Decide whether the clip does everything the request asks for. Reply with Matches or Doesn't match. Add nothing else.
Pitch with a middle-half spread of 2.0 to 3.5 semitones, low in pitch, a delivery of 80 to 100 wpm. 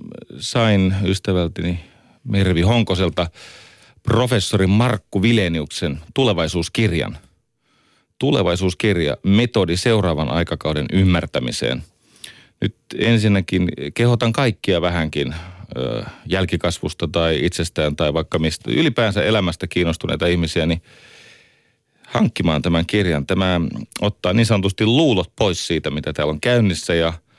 Doesn't match